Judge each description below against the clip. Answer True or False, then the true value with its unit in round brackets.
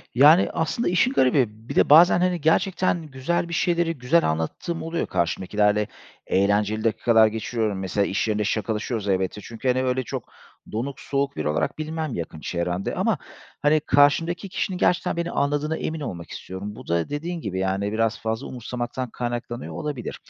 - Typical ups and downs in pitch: False (7.1 semitones)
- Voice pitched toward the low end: True (125 Hz)